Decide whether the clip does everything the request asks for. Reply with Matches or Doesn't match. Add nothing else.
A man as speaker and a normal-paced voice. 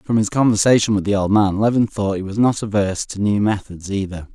Doesn't match